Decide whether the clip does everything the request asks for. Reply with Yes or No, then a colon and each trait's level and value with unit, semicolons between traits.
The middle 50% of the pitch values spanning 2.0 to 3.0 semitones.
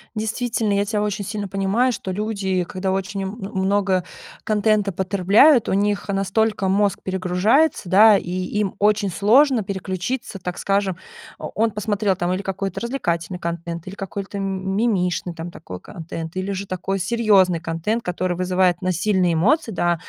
Yes: narrow, 2.4 semitones